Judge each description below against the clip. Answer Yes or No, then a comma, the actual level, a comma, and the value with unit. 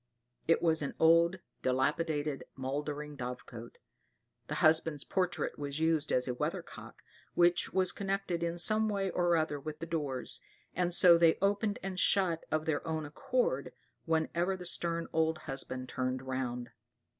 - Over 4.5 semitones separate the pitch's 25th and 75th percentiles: No, average, 3.6 semitones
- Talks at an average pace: Yes, average, 155 wpm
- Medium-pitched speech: Yes, medium, 160 Hz